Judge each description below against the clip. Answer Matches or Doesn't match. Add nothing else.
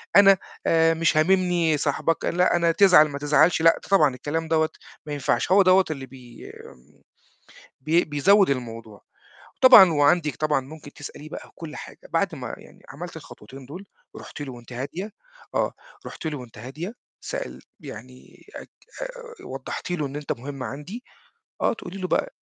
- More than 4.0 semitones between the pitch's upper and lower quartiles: Matches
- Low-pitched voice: Doesn't match